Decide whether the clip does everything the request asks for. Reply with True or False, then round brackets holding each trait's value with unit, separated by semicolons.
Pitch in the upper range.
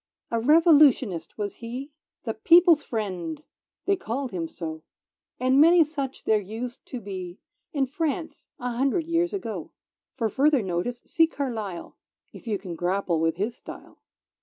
True (240 Hz)